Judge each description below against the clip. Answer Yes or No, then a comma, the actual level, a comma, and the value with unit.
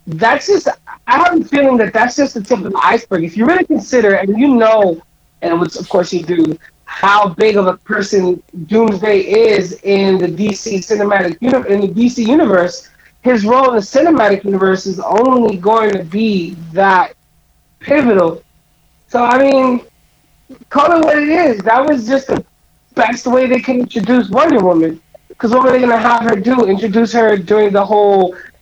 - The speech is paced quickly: No, average, 180 wpm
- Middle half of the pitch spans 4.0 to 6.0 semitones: Yes, average, 4.8 semitones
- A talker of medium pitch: No, high, 220 Hz